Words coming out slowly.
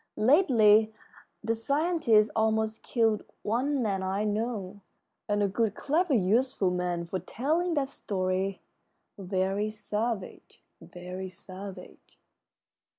Yes: slow, 105 wpm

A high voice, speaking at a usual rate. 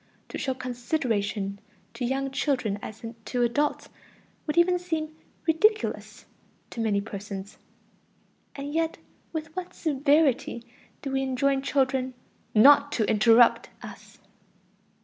No: very high, 270 Hz; slow, 115 wpm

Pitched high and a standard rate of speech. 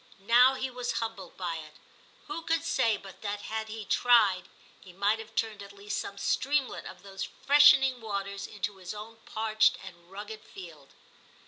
Yes: high, 210 Hz; average, 170 wpm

